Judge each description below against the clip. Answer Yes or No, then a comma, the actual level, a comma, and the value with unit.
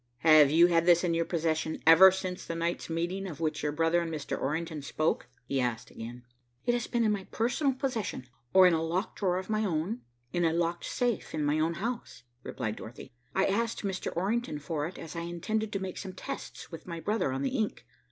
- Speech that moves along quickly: Yes, fast, 220 wpm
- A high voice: No, medium, 170 Hz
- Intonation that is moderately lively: Yes, average, 3.7 semitones